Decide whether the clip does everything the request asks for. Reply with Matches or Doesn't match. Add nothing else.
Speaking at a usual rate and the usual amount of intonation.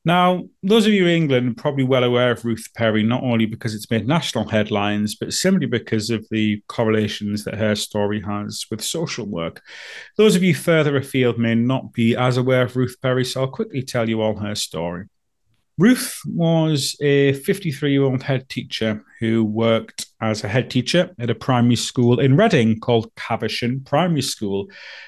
Matches